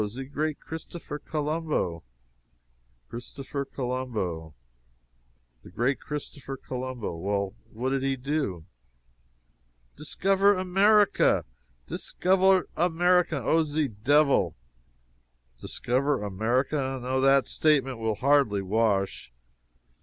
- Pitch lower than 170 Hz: Yes, low, 135 Hz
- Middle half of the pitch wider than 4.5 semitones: Yes, wide, 5.4 semitones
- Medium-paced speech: No, slow, 90 wpm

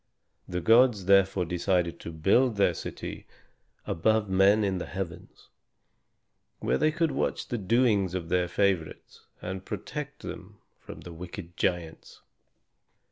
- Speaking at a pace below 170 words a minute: Yes, slow, 135 wpm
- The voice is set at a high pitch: No, very low, 95 Hz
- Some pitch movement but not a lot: Yes, average, 3.6 semitones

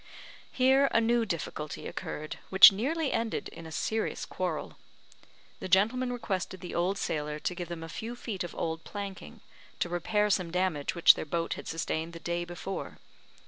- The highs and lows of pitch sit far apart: No, average, 5.0 semitones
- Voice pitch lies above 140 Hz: Yes, medium, 185 Hz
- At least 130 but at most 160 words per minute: No, average, 175 wpm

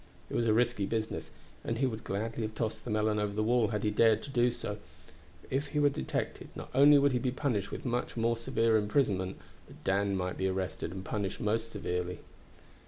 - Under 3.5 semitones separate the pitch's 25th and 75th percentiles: Yes, average, 3.1 semitones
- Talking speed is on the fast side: Yes, fast, 220 wpm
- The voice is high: No, low, 110 Hz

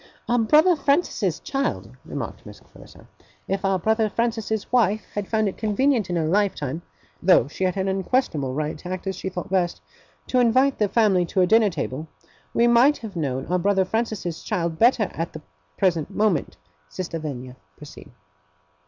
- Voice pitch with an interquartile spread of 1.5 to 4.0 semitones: No, average, 4.8 semitones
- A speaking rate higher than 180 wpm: No, average, 175 wpm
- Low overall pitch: No, high, 195 Hz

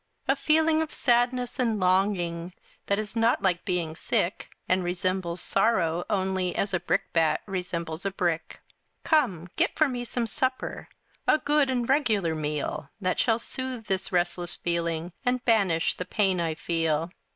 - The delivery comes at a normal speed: Yes, average, 155 wpm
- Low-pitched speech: No, high, 190 Hz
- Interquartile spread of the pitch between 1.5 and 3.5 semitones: No, wide, 5.6 semitones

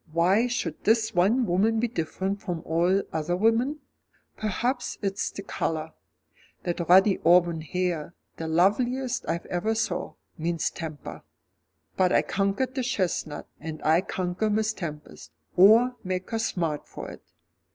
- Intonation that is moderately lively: Yes, average, 4.8 semitones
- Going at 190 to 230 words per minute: No, average, 140 wpm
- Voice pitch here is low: No, medium, 185 Hz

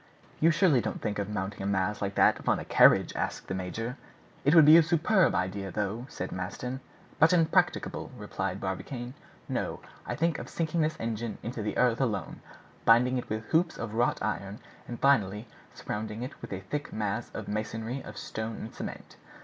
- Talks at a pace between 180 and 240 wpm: Yes, average, 190 wpm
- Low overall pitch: Yes, low, 115 Hz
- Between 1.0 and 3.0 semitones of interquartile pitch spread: No, average, 5.1 semitones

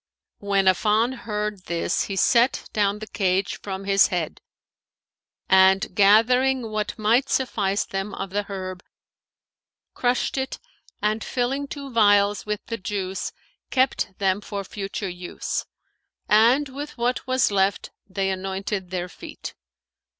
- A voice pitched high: Yes, high, 205 Hz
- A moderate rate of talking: No, slow, 130 wpm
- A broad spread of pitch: No, average, 3.4 semitones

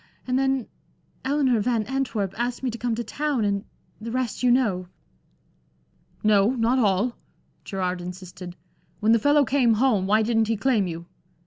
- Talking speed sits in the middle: Yes, average, 160 wpm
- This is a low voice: No, high, 230 Hz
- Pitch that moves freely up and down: No, average, 4.2 semitones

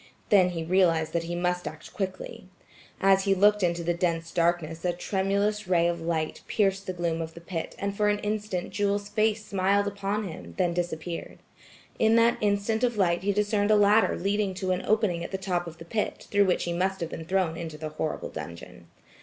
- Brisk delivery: Yes, fast, 210 wpm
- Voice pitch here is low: No, medium, 185 Hz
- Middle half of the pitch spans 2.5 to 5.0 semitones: Yes, average, 3.1 semitones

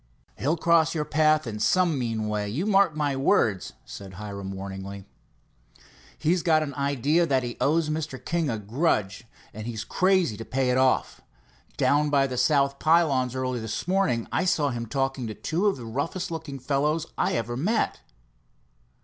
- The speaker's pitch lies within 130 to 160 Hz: Yes, medium, 140 Hz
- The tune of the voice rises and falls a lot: Yes, wide, 5.7 semitones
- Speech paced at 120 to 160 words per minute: No, average, 175 wpm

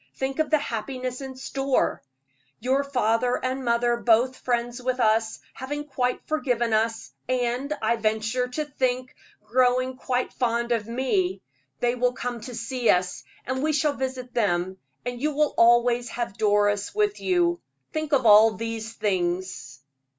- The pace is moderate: Yes, average, 155 wpm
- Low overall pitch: No, high, 245 Hz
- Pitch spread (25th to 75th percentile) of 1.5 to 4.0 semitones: Yes, narrow, 2.6 semitones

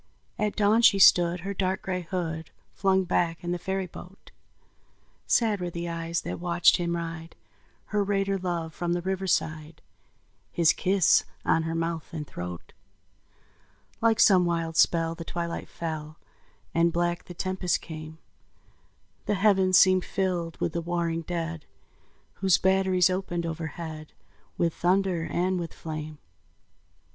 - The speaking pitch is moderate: Yes, medium, 175 Hz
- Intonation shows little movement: Yes, narrow, 2.3 semitones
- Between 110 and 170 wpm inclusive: Yes, average, 140 wpm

